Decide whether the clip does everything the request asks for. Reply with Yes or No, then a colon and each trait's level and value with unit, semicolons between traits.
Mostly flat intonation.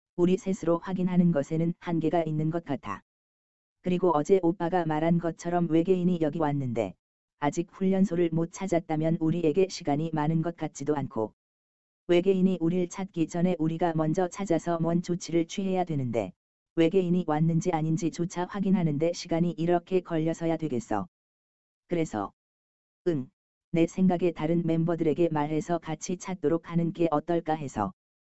Yes: narrow, 2.2 semitones